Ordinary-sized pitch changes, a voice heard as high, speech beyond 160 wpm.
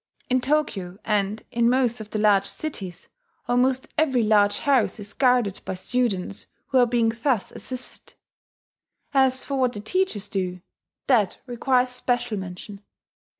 No: average, 3.9 semitones; high, 235 Hz; average, 145 wpm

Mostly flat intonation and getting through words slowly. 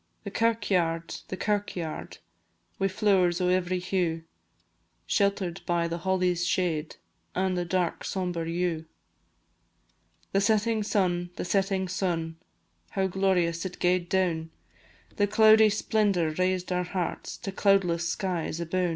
Yes: narrow, 2.2 semitones; slow, 125 wpm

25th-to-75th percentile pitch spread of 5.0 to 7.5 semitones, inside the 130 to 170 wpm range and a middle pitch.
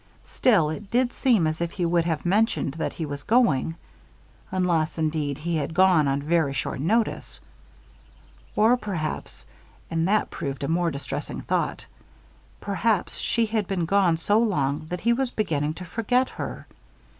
Yes: average, 5.3 semitones; average, 160 wpm; medium, 170 Hz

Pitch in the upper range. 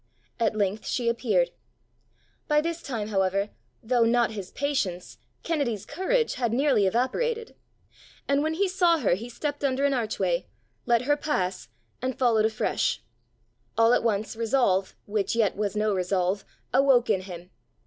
Yes: high, 235 Hz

